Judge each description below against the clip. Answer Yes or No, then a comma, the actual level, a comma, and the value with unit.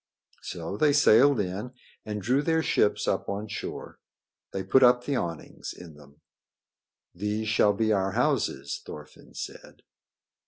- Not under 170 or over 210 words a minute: No, average, 145 wpm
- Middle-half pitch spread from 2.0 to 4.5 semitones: No, average, 5.3 semitones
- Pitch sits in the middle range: No, low, 105 Hz